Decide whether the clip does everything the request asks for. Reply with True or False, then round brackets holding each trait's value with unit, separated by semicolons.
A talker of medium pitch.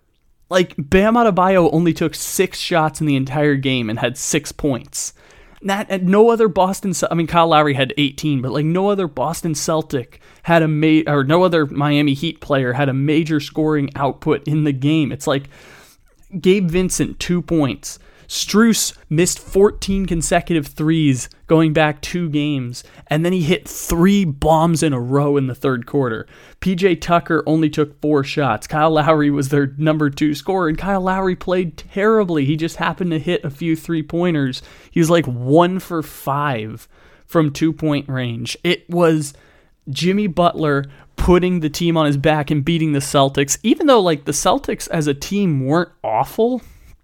True (155 Hz)